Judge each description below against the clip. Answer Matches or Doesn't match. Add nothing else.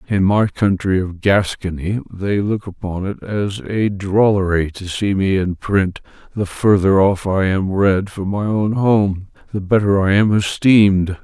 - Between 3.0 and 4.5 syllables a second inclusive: Matches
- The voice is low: Matches